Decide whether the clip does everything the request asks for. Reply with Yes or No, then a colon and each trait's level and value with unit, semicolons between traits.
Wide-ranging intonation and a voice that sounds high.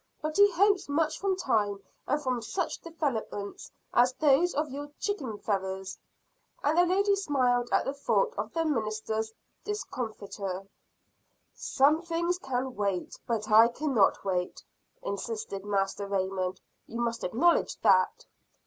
Yes: wide, 7.5 semitones; high, 245 Hz